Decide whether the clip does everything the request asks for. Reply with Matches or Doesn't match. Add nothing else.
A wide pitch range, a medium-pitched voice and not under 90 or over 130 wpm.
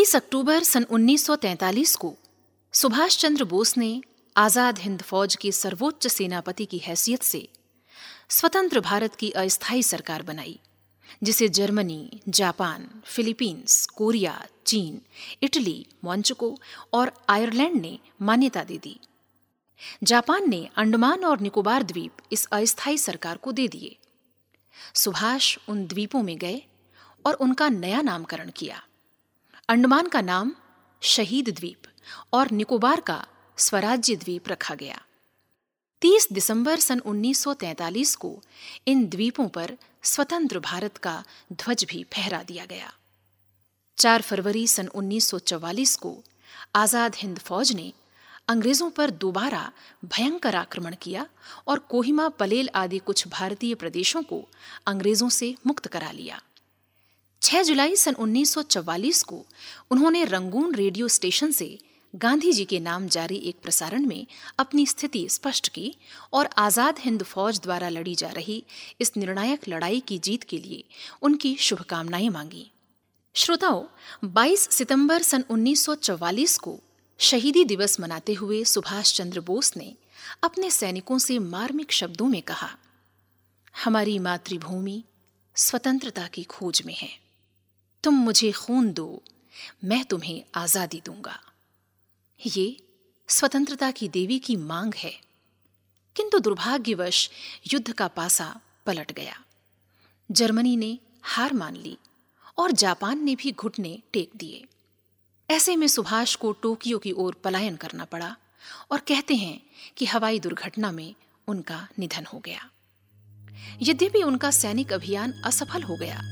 Doesn't match